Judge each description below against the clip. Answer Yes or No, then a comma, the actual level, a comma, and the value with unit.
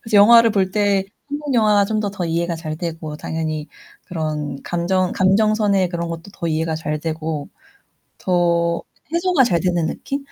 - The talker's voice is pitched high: No, medium, 175 Hz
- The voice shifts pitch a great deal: No, average, 4.2 semitones